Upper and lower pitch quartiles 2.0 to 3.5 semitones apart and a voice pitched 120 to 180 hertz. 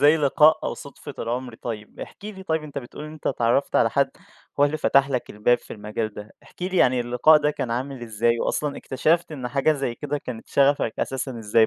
No: average, 4.0 semitones; low, 135 Hz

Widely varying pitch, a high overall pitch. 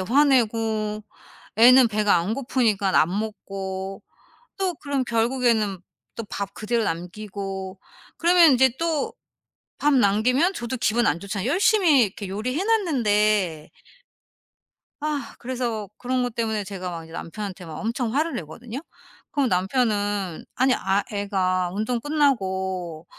No: average, 4.9 semitones; high, 220 Hz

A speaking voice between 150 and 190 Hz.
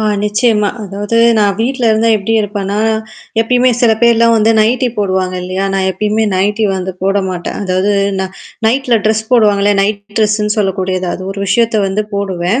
No: high, 205 Hz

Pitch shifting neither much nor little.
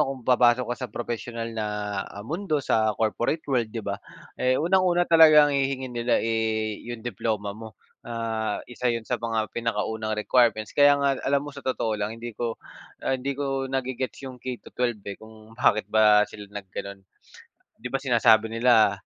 Yes: average, 3.2 semitones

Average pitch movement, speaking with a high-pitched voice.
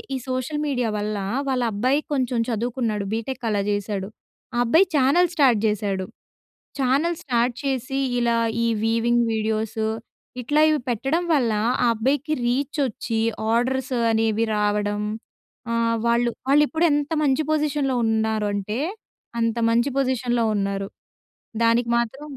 Yes: average, 3.5 semitones; high, 240 Hz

